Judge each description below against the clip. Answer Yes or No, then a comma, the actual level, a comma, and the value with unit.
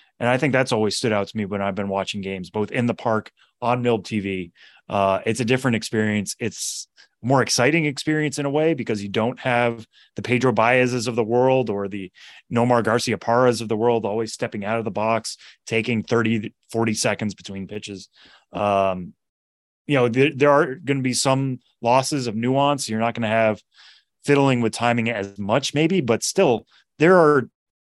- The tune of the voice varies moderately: Yes, average, 3.4 semitones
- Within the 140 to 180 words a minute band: No, average, 190 wpm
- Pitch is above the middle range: No, low, 115 Hz